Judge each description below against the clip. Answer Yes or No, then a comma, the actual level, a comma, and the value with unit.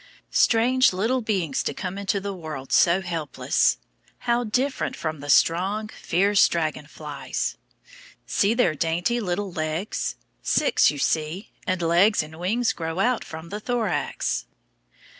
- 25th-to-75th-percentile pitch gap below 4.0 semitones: No, average, 5.1 semitones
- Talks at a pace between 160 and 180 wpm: No, average, 140 wpm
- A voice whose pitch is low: No, medium, 180 Hz